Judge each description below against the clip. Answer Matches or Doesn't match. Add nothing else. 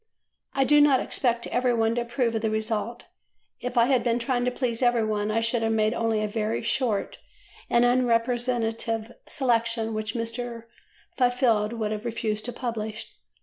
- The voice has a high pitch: Matches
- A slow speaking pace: Doesn't match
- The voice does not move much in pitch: Matches